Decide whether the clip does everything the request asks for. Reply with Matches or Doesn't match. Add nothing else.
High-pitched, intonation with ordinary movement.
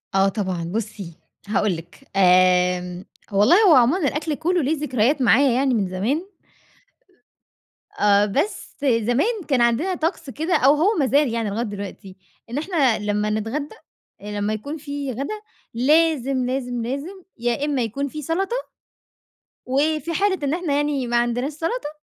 Doesn't match